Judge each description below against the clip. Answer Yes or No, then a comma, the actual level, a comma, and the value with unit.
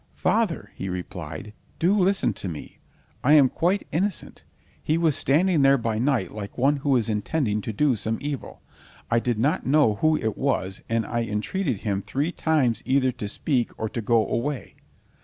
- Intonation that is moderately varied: No, wide, 5.7 semitones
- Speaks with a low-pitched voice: Yes, low, 130 Hz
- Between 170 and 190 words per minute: Yes, average, 180 wpm